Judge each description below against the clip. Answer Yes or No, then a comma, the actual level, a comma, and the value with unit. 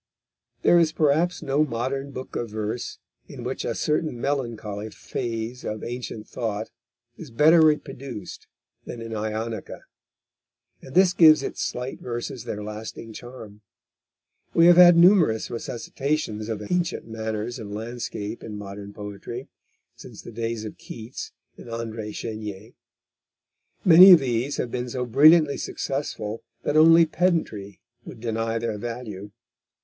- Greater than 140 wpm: No, slow, 135 wpm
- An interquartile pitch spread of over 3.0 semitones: Yes, average, 4.8 semitones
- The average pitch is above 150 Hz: No, low, 120 Hz